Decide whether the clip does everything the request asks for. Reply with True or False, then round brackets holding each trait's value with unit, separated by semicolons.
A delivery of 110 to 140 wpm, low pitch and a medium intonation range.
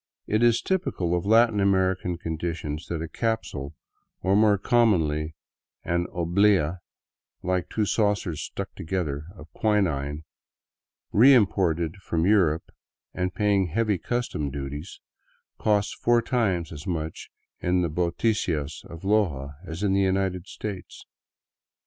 True (135 wpm; 90 Hz; 4.4 semitones)